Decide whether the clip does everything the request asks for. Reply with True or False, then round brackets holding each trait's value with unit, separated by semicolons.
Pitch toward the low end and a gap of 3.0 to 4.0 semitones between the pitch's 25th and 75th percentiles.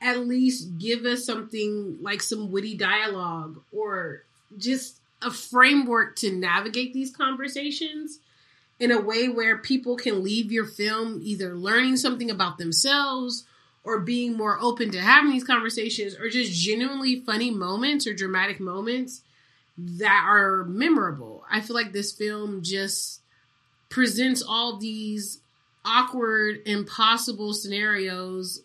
False (220 Hz; 3.7 semitones)